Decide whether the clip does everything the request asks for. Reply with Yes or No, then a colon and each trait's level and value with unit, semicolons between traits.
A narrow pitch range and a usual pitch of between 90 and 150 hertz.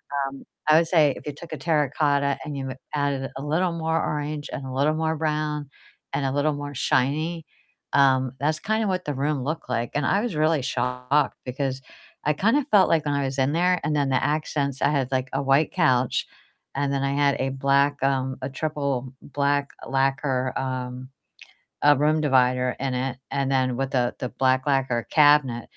Yes: narrow, 2.3 semitones; medium, 140 Hz